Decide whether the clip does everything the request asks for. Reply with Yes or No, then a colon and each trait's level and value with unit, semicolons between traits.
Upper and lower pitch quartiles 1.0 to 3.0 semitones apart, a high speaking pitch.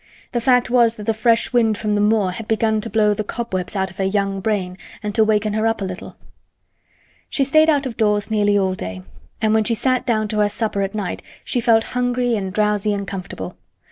Yes: narrow, 2.4 semitones; high, 215 Hz